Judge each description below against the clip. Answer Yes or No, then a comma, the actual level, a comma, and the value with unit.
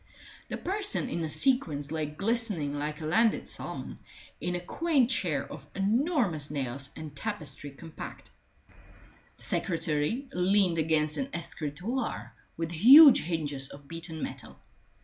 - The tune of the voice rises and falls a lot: Yes, wide, 7.2 semitones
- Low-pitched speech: No, medium, 165 Hz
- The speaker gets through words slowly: Yes, slow, 130 wpm